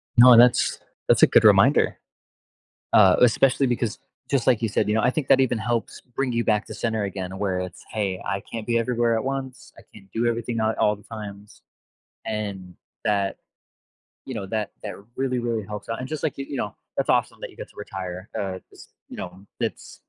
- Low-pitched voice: Yes, low, 110 Hz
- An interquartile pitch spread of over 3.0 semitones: Yes, average, 3.5 semitones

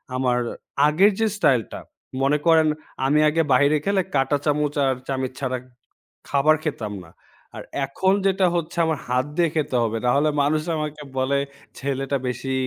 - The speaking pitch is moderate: Yes, medium, 145 Hz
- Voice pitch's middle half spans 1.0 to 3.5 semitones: Yes, average, 2.9 semitones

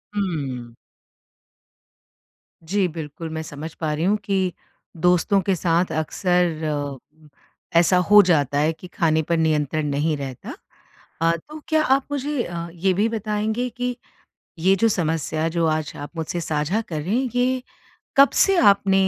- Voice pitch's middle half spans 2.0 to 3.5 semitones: No, average, 4.8 semitones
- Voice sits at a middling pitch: Yes, medium, 170 Hz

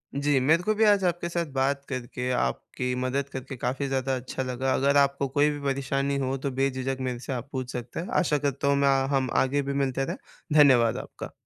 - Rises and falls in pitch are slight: Yes, narrow, 1.6 semitones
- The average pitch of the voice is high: No, low, 135 Hz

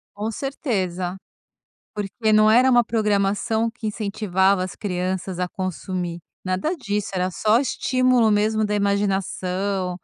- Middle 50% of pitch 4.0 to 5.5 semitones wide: No, average, 2.8 semitones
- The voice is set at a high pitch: Yes, high, 205 Hz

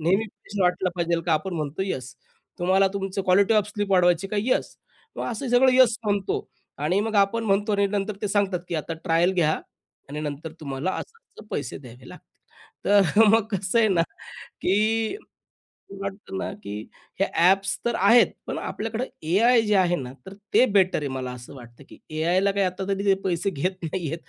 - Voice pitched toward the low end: No, high, 190 Hz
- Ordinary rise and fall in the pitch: Yes, average, 3.7 semitones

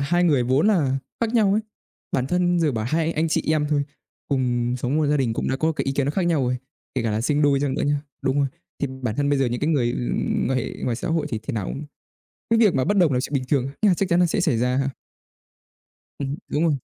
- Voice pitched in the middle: Yes, medium, 145 Hz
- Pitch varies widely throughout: No, average, 4.1 semitones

